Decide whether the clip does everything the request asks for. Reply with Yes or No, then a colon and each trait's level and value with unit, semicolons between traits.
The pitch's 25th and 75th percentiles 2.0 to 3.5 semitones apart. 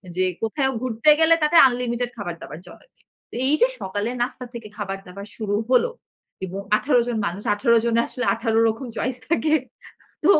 No: average, 4.0 semitones